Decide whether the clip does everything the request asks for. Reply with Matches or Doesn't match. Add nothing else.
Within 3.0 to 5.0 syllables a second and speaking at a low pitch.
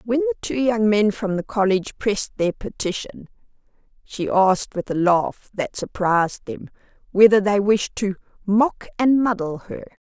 Doesn't match